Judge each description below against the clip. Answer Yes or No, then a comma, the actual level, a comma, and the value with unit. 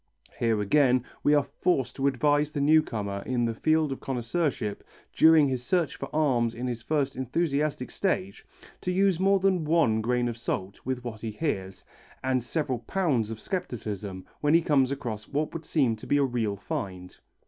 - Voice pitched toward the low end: Yes, low, 130 Hz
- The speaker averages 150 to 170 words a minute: No, average, 185 wpm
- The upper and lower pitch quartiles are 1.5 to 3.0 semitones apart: No, average, 5.2 semitones